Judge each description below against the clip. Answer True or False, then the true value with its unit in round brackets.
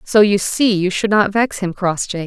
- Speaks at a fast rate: True (240 wpm)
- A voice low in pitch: False (200 Hz)